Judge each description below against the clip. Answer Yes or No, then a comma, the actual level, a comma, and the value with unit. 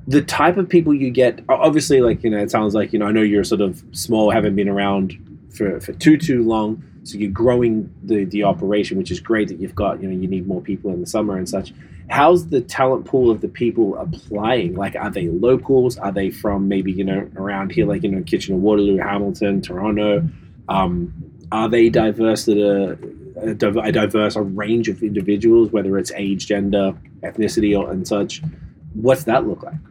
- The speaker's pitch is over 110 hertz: No, low, 105 Hz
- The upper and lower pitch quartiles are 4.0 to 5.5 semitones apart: No, average, 3.1 semitones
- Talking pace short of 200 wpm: No, fast, 205 wpm